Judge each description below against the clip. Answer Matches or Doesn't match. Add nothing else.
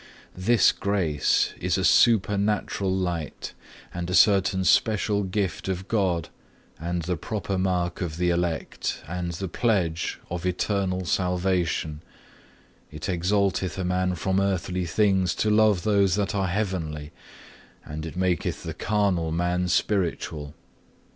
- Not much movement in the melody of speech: Matches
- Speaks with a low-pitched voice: Matches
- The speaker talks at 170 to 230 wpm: Doesn't match